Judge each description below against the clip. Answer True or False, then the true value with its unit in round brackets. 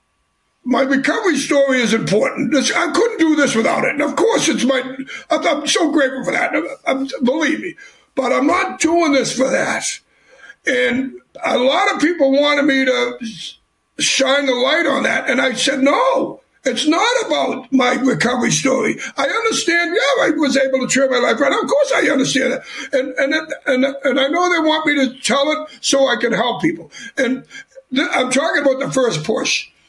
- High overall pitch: True (270 Hz)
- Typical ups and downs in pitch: True (3.2 semitones)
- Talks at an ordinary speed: True (185 wpm)